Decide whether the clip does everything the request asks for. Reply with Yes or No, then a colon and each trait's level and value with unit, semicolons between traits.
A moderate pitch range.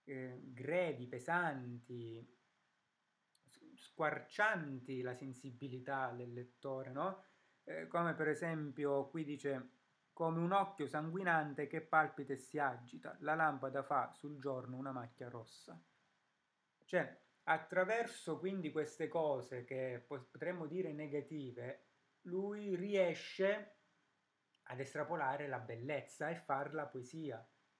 Yes: average, 4.0 semitones